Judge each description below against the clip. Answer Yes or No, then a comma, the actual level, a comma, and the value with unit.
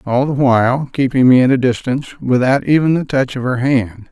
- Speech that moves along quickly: Yes, fast, 220 wpm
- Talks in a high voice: No, low, 130 Hz